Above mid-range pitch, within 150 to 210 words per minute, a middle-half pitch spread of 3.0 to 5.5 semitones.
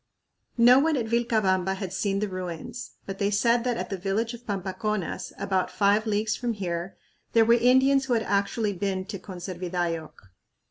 Yes: high, 200 Hz; average, 175 wpm; average, 3.7 semitones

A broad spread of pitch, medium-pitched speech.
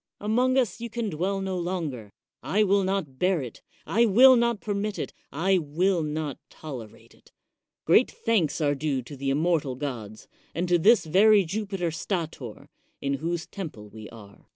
Yes: wide, 5.8 semitones; medium, 175 Hz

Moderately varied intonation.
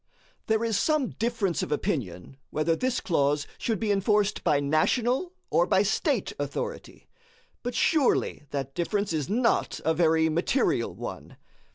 No: wide, 7.3 semitones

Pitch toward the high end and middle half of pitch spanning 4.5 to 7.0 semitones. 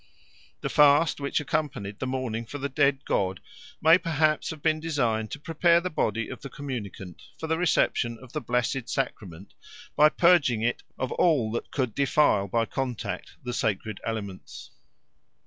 No: low, 130 Hz; average, 5.2 semitones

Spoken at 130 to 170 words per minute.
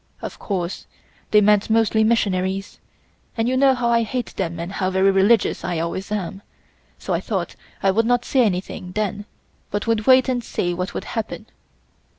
No: average, 180 wpm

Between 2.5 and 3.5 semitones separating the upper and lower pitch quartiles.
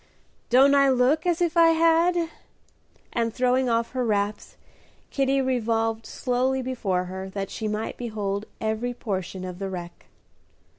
No: average, 4.4 semitones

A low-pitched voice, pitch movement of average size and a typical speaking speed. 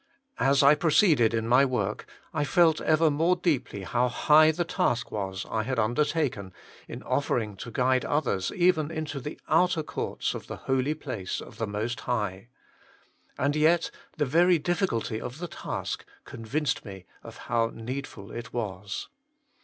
No: low, 130 Hz; wide, 5.7 semitones; average, 160 wpm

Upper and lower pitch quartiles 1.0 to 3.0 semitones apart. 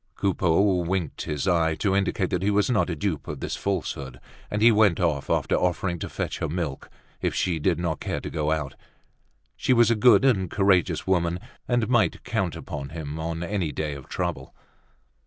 No: average, 3.9 semitones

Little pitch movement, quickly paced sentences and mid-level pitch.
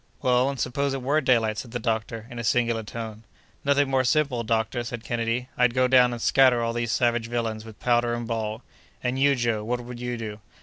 No: narrow, 1.8 semitones; fast, 220 wpm; low, 120 Hz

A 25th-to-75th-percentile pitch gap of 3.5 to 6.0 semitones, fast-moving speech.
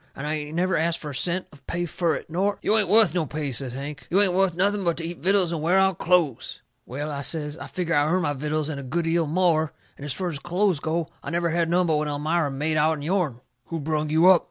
No: average, 3.0 semitones; fast, 275 wpm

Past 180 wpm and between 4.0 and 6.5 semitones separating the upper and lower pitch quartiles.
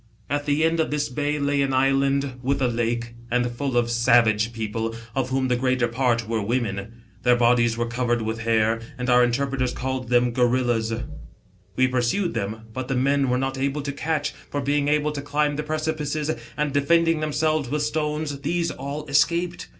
No: average, 190 wpm; average, 3.6 semitones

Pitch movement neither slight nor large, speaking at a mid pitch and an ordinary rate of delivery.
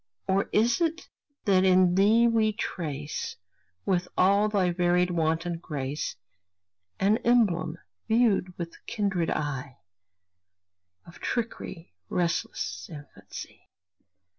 No: average, 4.4 semitones; medium, 180 Hz; slow, 100 wpm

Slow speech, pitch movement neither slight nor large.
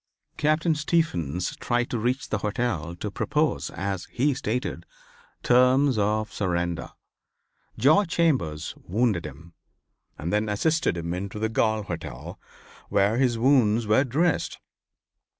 No: slow, 125 wpm; wide, 6.0 semitones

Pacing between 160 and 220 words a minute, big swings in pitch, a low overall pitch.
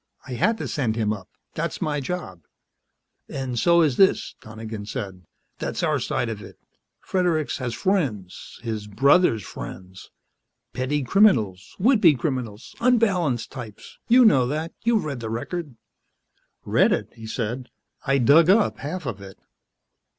No: average, 150 wpm; wide, 7.6 semitones; low, 130 Hz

